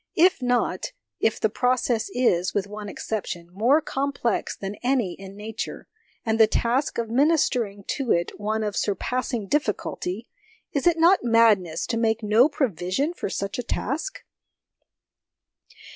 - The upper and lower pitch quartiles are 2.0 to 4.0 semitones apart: No, average, 4.5 semitones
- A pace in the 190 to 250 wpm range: No, average, 145 wpm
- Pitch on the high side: Yes, high, 225 Hz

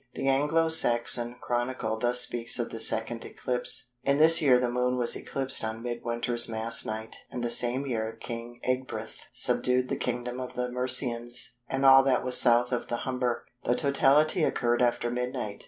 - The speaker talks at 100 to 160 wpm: No, average, 175 wpm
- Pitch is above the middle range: No, low, 125 Hz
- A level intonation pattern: Yes, narrow, 1.5 semitones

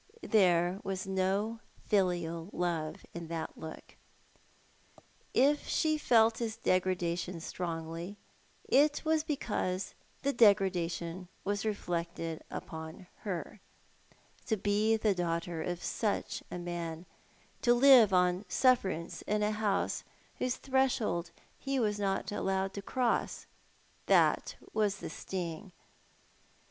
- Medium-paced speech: No, slow, 115 wpm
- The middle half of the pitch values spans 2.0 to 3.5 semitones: No, average, 4.1 semitones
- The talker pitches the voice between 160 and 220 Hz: Yes, high, 190 Hz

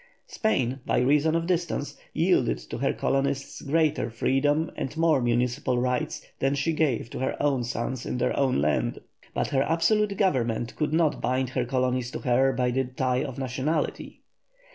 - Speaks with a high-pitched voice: No, low, 135 Hz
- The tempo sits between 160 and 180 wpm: Yes, average, 170 wpm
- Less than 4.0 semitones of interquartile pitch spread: Yes, average, 3.4 semitones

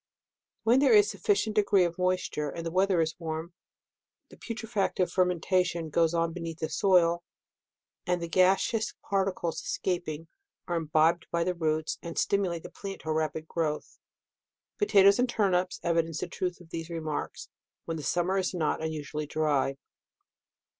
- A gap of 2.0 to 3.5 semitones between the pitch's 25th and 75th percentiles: Yes, average, 2.8 semitones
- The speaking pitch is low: No, medium, 170 Hz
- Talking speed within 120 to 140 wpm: No, average, 165 wpm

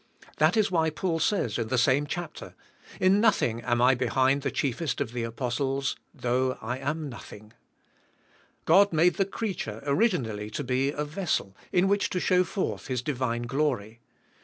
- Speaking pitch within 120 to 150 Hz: Yes, low, 135 Hz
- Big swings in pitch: Yes, wide, 6.3 semitones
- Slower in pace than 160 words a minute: No, average, 170 wpm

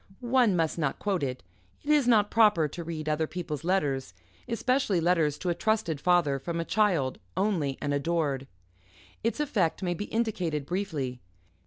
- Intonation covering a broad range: Yes, wide, 5.7 semitones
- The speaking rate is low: No, average, 165 wpm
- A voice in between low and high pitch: Yes, medium, 170 Hz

